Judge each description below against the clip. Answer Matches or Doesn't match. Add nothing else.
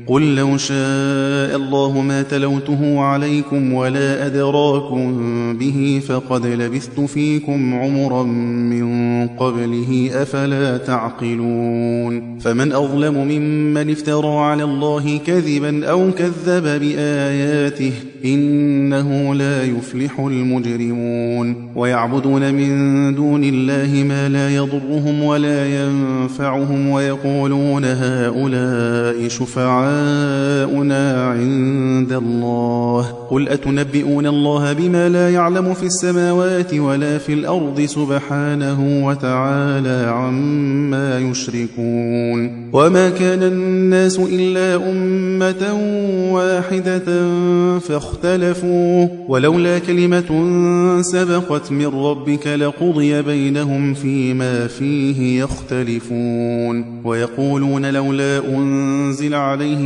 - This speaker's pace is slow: Matches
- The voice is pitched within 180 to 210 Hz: Doesn't match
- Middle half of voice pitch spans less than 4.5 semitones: Matches